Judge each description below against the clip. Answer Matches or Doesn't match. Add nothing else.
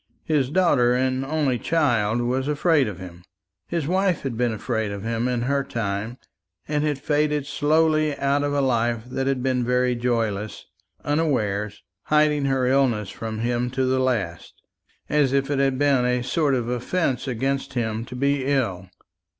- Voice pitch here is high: Doesn't match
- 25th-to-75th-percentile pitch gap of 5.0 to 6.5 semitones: Doesn't match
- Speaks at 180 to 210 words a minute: Doesn't match